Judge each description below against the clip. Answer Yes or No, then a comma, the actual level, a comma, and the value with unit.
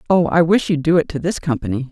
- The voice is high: No, medium, 155 Hz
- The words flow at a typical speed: No, fast, 280 wpm